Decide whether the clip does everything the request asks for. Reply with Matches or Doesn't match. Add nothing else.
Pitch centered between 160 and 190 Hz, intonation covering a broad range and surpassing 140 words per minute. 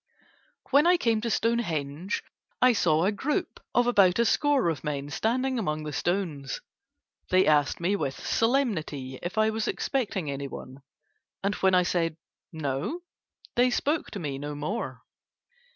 Matches